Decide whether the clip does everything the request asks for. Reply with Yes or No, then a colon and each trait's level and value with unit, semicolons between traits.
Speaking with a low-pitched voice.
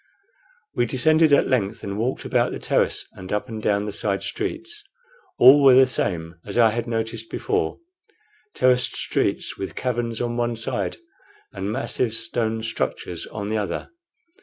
Yes: low, 115 Hz